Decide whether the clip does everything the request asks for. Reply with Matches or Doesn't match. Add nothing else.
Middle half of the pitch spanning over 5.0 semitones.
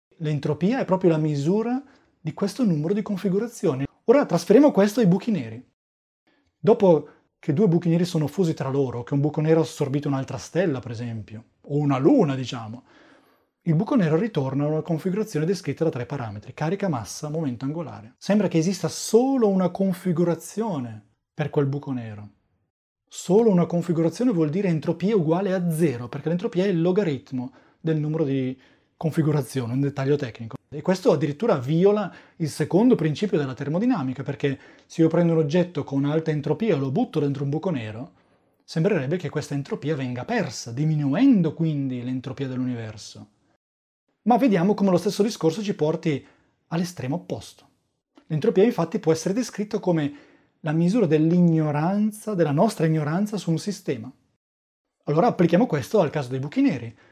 Matches